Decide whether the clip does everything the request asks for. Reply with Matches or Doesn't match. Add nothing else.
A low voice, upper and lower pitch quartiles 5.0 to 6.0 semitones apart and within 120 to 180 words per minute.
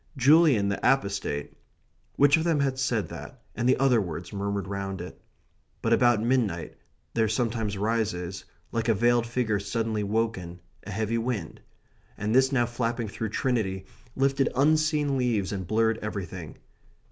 Doesn't match